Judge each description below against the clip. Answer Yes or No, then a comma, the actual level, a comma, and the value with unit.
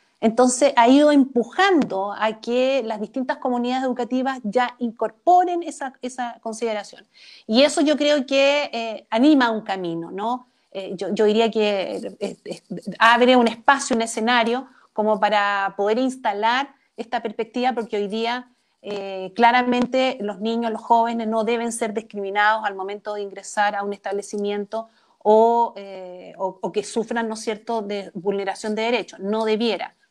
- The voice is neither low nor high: No, high, 230 Hz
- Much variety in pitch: No, average, 3.3 semitones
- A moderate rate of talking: Yes, average, 155 wpm